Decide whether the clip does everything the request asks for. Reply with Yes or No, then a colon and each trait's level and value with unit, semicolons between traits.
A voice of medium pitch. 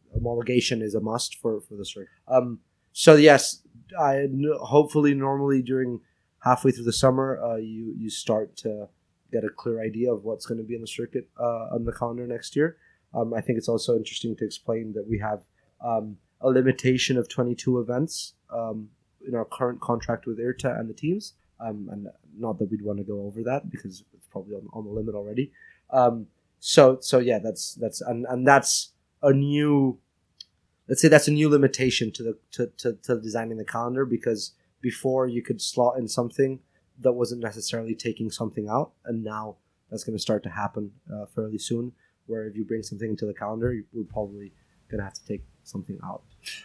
No: low, 115 Hz